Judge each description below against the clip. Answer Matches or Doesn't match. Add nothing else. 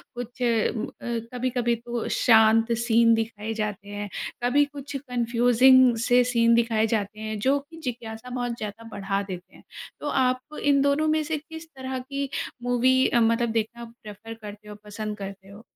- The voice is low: Doesn't match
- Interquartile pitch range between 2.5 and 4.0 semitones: Matches